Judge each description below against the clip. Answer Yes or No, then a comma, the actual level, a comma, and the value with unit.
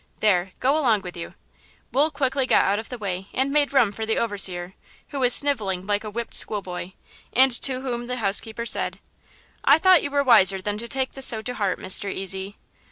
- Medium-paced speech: No, fast, 210 wpm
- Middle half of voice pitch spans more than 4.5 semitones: Yes, average, 5.2 semitones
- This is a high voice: Yes, high, 225 Hz